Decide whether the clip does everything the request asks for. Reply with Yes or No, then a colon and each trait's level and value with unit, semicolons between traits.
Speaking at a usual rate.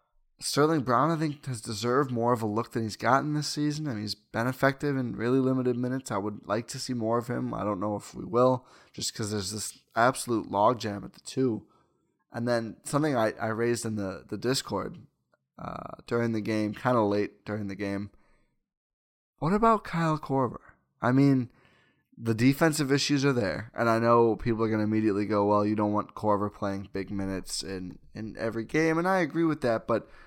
No: fast, 210 wpm